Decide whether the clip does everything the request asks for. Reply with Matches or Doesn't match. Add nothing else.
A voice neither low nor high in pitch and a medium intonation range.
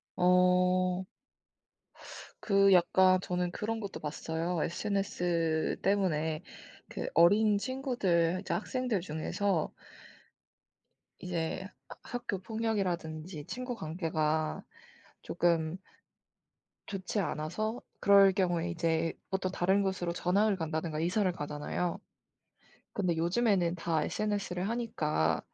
Matches